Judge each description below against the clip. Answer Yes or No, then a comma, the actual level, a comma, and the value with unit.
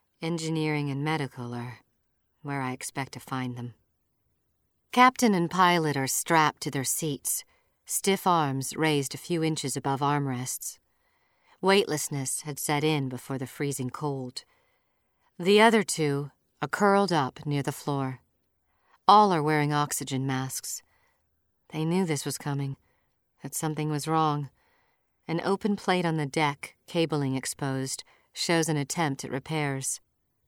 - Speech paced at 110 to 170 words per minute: Yes, average, 140 wpm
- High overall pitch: No, medium, 145 Hz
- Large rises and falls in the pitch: No, average, 3.6 semitones